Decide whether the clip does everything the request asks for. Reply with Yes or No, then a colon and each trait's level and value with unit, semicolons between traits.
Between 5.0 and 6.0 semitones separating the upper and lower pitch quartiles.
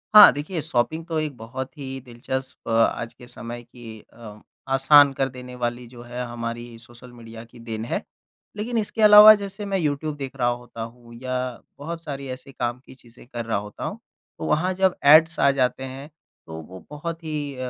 No: average, 4.3 semitones